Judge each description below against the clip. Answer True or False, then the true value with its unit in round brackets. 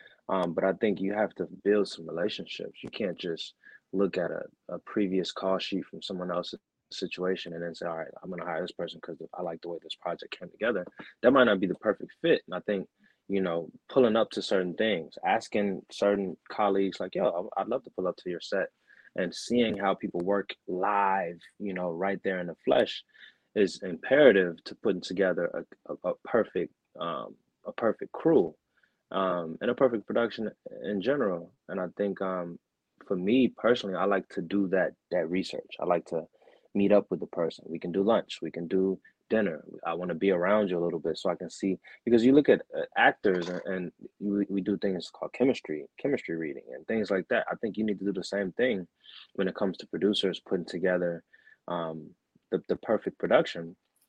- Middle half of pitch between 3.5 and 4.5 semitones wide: False (2.4 semitones)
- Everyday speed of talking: False (210 wpm)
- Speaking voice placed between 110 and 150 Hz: False (95 Hz)